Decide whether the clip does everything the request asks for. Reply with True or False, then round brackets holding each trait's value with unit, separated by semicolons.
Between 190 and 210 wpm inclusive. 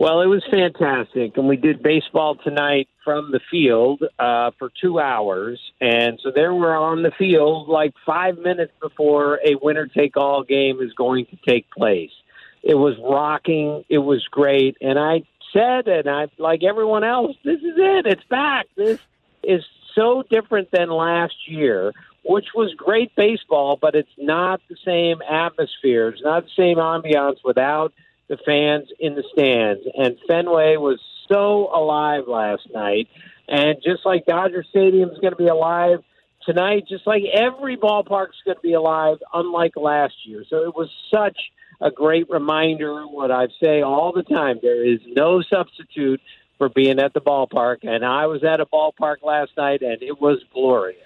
False (175 wpm)